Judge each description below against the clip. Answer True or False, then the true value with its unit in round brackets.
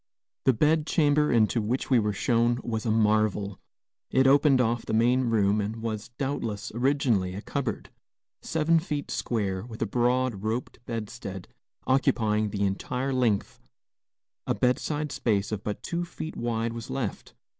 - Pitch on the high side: False (115 Hz)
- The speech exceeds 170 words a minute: False (155 wpm)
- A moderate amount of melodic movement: True (3.7 semitones)